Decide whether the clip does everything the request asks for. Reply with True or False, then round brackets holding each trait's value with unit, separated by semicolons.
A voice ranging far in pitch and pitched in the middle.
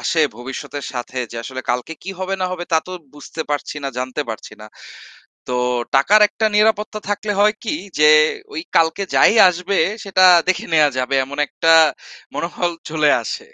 True (5.7 semitones; 160 Hz)